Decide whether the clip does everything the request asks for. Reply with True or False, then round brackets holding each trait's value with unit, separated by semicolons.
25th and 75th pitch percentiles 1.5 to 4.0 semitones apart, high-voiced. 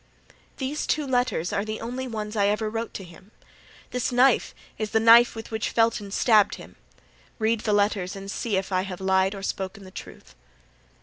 True (2.9 semitones; 215 Hz)